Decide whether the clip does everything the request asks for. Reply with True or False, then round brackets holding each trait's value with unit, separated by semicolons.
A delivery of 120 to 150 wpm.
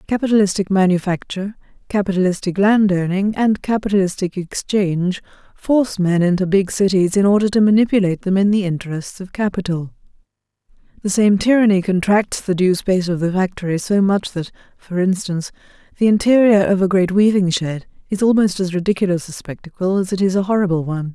False (160 wpm)